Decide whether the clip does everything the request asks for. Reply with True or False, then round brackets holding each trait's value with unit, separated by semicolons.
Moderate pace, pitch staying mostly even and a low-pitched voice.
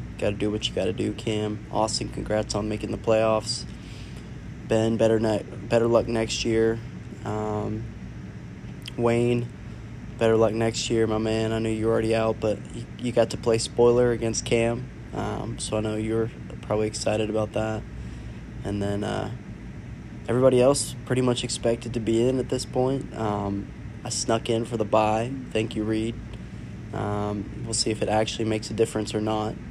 True (180 wpm; 1.4 semitones; 110 Hz)